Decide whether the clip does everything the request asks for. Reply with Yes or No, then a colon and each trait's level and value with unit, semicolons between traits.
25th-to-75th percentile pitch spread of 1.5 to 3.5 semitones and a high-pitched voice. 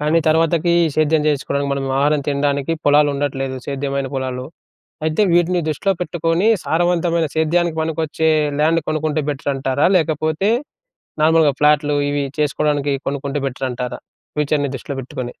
No: narrow, 2.4 semitones; medium, 150 Hz